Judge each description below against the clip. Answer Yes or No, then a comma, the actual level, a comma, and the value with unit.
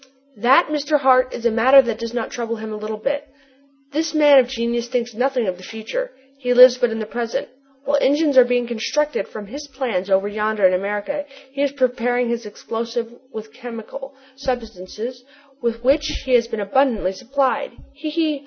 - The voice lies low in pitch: No, high, 245 Hz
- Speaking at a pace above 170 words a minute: Yes, average, 190 wpm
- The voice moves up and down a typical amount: Yes, average, 3.5 semitones